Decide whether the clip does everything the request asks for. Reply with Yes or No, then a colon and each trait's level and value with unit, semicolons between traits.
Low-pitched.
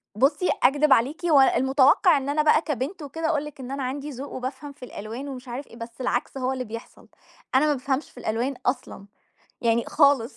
No: very high, 270 Hz